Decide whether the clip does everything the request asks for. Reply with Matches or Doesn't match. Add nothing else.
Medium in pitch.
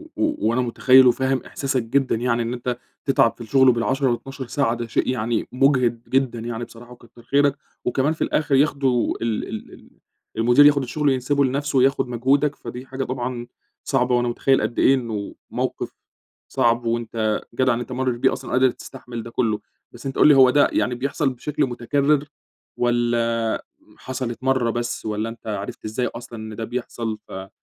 Doesn't match